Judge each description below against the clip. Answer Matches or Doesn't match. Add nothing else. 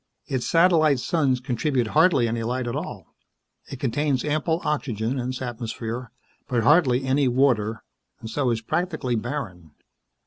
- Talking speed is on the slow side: Doesn't match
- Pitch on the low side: Matches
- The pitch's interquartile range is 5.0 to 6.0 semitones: Doesn't match